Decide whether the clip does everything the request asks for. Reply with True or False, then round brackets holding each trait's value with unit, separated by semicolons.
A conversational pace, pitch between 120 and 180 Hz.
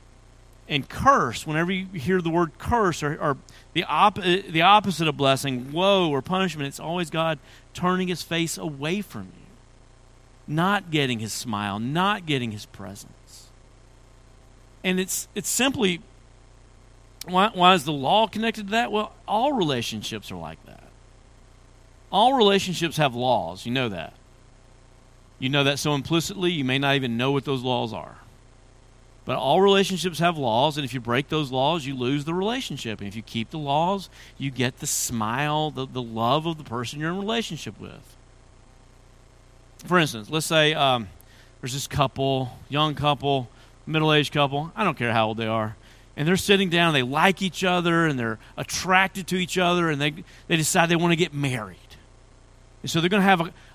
True (180 wpm; 140 Hz)